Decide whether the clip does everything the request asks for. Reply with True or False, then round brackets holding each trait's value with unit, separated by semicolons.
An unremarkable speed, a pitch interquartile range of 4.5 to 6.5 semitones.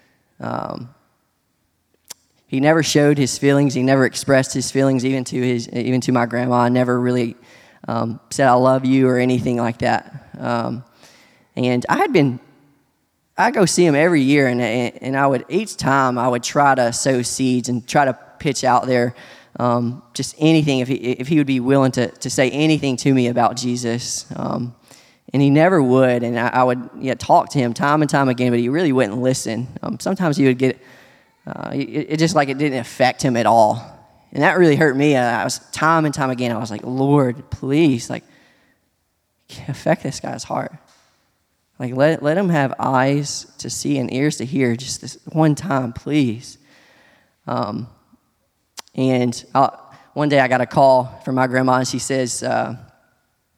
False (190 wpm; 2.4 semitones)